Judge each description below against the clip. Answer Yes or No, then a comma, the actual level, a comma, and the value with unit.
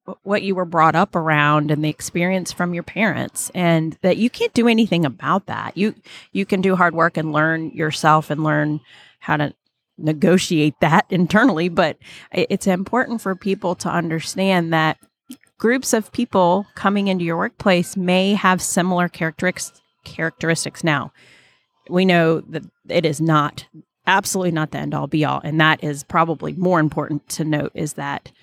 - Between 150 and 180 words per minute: Yes, average, 170 wpm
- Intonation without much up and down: No, average, 3.5 semitones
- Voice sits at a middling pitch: Yes, medium, 175 Hz